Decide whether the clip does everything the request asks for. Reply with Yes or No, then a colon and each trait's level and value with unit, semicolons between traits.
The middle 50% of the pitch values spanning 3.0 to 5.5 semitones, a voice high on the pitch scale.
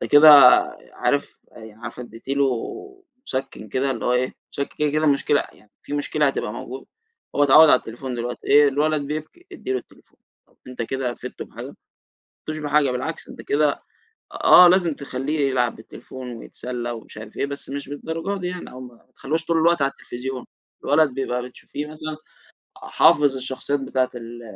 No: average, 3.5 semitones; low, 135 Hz